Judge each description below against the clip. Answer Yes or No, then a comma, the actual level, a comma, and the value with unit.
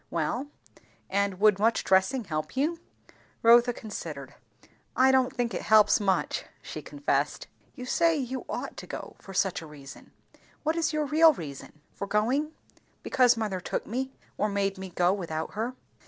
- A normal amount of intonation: No, wide, 5.7 semitones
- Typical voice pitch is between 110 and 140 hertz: No, high, 215 Hz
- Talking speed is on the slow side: No, average, 165 wpm